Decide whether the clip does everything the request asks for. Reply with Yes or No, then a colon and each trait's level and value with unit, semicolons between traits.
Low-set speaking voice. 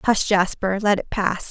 No: high, 200 Hz